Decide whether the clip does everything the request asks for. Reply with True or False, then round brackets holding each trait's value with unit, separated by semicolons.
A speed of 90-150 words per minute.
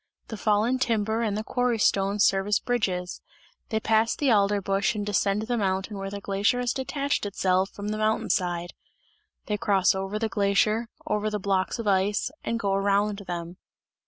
False (185 wpm)